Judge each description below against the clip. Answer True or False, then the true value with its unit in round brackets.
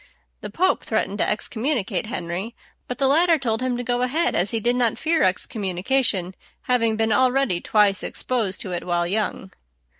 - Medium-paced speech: True (175 wpm)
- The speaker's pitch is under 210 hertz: False (225 Hz)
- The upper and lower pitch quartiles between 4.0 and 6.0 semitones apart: True (4.8 semitones)